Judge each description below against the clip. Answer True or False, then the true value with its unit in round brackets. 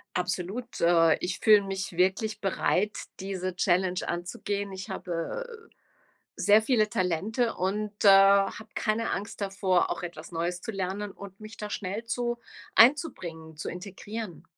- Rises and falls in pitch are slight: False (3.0 semitones)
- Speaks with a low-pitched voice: False (195 Hz)